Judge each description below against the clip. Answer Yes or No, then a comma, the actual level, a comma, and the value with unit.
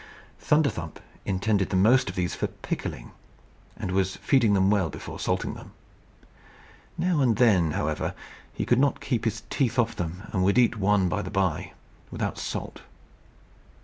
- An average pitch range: Yes, average, 4.5 semitones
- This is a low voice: Yes, low, 100 Hz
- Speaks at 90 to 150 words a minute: No, average, 160 wpm